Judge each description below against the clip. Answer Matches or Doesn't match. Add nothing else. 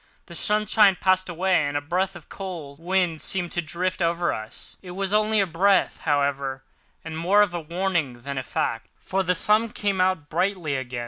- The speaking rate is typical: Doesn't match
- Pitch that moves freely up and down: Doesn't match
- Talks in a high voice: Doesn't match